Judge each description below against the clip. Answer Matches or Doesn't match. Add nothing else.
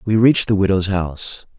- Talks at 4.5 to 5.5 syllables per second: Doesn't match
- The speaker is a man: Matches